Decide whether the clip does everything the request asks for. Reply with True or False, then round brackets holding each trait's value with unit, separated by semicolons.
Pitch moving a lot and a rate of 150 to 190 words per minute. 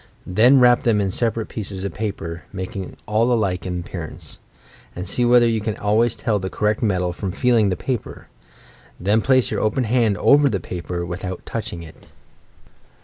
False (4.1 semitones; 180 wpm)